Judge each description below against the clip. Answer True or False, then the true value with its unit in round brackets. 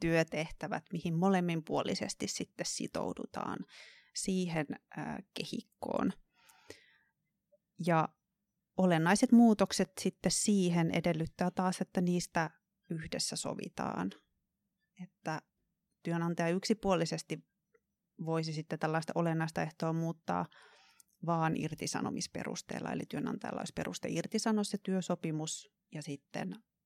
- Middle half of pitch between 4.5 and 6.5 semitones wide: False (3.2 semitones)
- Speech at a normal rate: False (85 wpm)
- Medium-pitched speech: True (180 Hz)